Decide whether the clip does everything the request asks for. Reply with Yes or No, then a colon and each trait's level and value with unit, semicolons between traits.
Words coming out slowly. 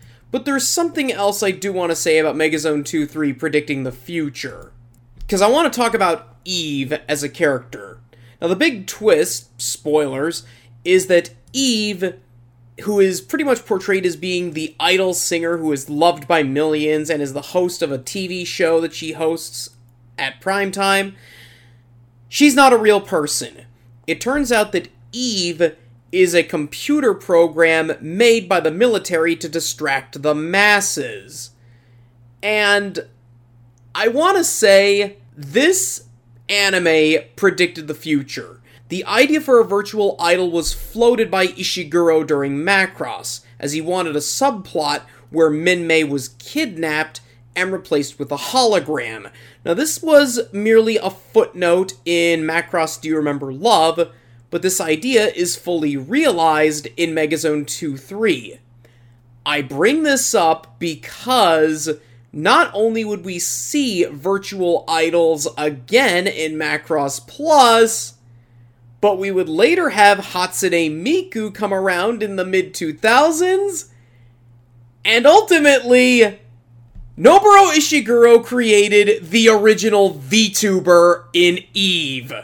Yes: slow, 130 wpm